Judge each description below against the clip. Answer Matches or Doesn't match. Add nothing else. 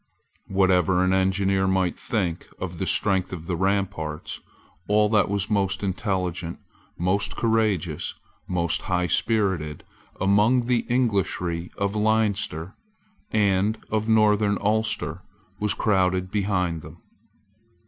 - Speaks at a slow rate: Matches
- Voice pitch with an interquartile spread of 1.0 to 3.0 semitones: Matches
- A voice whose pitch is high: Doesn't match